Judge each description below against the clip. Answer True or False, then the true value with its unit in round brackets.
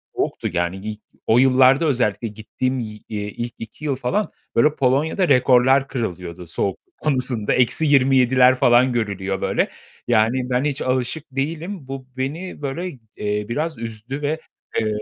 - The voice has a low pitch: True (125 Hz)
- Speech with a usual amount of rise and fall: True (4.0 semitones)